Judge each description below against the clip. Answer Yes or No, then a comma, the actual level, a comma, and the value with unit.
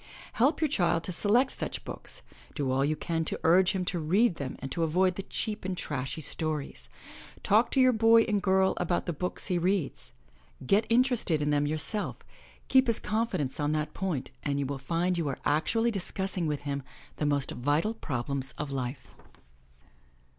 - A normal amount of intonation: No, wide, 5.9 semitones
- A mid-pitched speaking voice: Yes, medium, 170 Hz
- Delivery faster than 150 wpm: Yes, average, 185 wpm